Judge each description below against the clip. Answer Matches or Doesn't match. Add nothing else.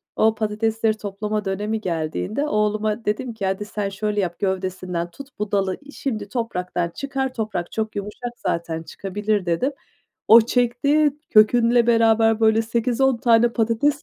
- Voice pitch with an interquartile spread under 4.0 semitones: Matches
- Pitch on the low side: Doesn't match